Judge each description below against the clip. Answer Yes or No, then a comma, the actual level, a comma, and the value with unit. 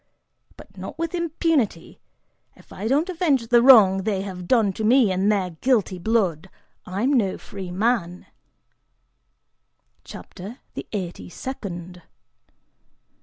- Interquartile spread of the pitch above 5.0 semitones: Yes, wide, 5.6 semitones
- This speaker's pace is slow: Yes, slow, 120 wpm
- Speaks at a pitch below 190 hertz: No, high, 210 Hz